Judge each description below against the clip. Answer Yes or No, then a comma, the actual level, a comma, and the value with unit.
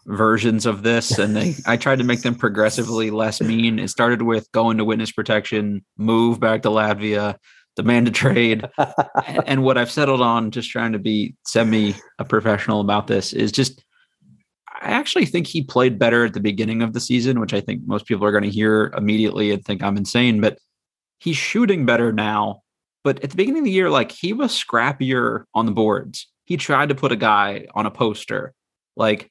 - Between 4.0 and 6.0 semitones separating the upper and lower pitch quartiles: No, average, 3.5 semitones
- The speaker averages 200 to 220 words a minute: Yes, fast, 205 wpm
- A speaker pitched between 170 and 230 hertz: No, low, 115 Hz